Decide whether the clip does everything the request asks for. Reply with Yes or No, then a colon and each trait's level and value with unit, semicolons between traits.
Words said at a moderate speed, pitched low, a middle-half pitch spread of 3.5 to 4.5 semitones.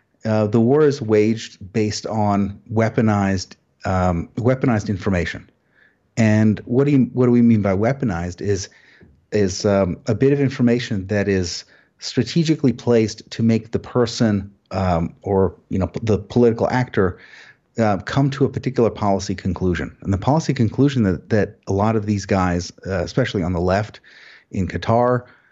Yes: average, 160 wpm; low, 110 Hz; average, 3.8 semitones